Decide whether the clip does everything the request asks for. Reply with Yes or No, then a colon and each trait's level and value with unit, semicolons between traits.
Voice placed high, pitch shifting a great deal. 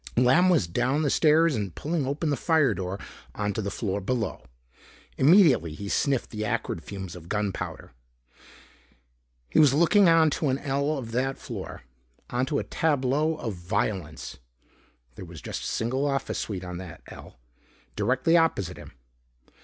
No: low, 125 Hz; wide, 7.2 semitones